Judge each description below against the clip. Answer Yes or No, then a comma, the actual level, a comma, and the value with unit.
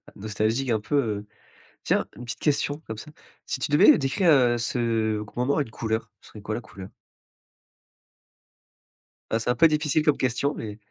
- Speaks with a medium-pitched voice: No, low, 120 Hz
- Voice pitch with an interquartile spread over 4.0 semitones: Yes, average, 4.5 semitones